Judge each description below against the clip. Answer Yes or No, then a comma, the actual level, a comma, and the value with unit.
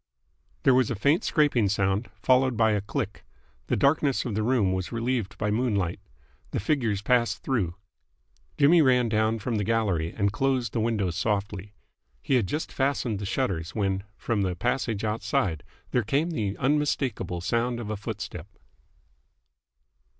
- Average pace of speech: Yes, average, 160 wpm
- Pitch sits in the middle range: No, low, 110 Hz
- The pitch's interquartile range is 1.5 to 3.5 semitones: No, average, 4.3 semitones